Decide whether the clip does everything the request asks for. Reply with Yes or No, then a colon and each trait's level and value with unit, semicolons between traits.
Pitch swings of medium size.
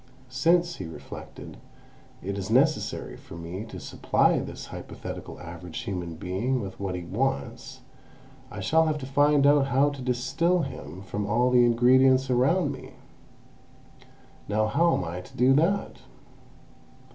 No: wide, 6.4 semitones